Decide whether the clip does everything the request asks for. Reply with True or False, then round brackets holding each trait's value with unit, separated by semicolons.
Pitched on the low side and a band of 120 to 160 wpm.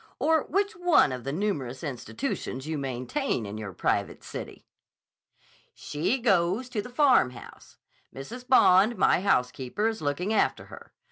False (180 Hz; 140 wpm)